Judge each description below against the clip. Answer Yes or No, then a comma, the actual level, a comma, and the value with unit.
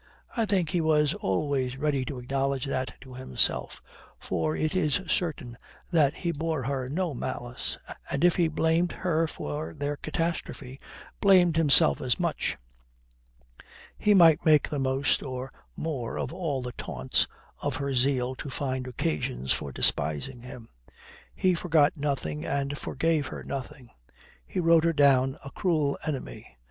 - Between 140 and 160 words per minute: Yes, average, 150 wpm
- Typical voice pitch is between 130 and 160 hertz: Yes, medium, 140 Hz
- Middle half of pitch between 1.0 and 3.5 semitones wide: No, average, 4.0 semitones